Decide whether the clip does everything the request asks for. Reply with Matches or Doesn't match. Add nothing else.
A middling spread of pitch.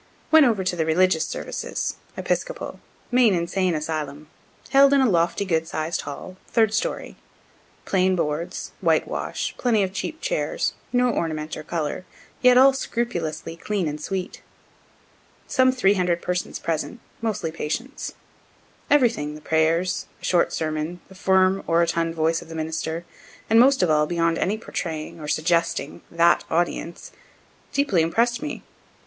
Doesn't match